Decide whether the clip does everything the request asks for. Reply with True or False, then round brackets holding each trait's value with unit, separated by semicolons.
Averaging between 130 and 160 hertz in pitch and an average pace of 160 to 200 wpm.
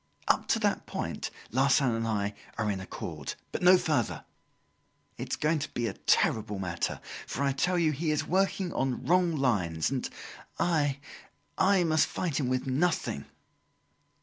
True (140 Hz; 165 wpm)